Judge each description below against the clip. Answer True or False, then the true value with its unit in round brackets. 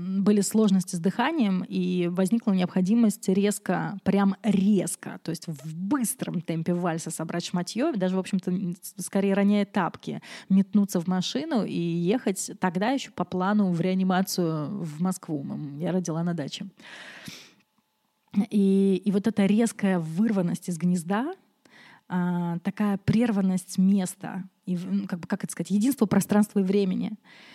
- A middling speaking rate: True (135 wpm)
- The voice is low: False (195 Hz)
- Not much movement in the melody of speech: True (2.3 semitones)